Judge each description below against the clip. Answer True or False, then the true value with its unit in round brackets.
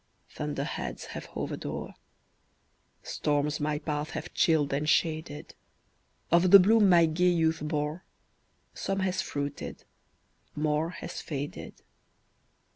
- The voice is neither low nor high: True (155 Hz)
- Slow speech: True (120 wpm)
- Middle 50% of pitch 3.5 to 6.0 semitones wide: False (2.8 semitones)